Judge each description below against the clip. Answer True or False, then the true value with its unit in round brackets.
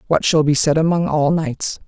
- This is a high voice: False (160 Hz)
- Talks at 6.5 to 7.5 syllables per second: False (4.9 syllables/s)